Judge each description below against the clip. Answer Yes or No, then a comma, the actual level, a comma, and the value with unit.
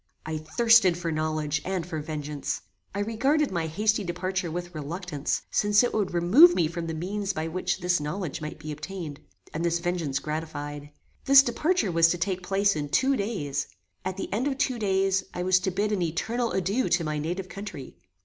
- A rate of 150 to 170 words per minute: No, average, 195 wpm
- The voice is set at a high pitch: No, medium, 180 Hz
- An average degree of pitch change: Yes, average, 4.6 semitones